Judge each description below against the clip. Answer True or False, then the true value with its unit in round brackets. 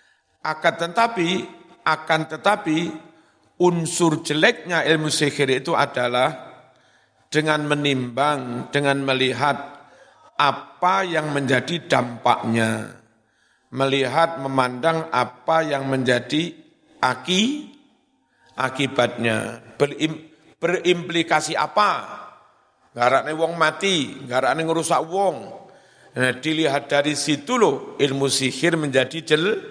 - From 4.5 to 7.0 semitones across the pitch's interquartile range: False (4.1 semitones)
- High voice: False (150 Hz)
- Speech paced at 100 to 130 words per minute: False (85 wpm)